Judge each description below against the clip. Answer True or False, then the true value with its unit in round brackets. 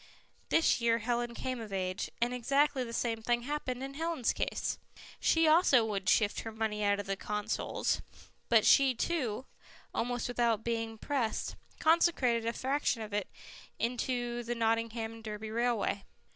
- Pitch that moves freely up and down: False (2.6 semitones)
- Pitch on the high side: True (235 Hz)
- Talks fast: False (155 wpm)